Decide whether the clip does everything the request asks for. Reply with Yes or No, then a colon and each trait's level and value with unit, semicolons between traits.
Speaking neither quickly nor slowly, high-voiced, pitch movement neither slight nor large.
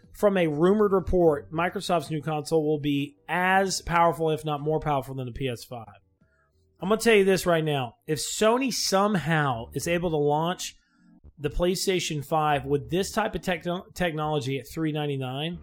No: average, 170 wpm; medium, 155 Hz; average, 4.0 semitones